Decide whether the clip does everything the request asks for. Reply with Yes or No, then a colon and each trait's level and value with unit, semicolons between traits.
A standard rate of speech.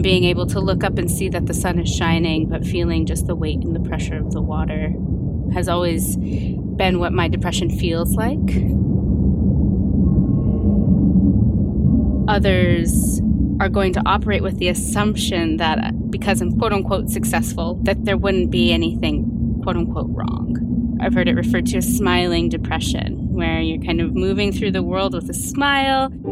Yes: average, 165 wpm